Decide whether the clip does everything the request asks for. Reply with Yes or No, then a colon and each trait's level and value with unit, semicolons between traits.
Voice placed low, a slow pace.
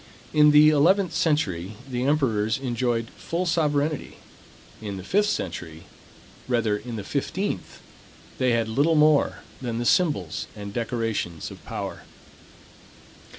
Yes: low, 125 Hz; slow, 105 wpm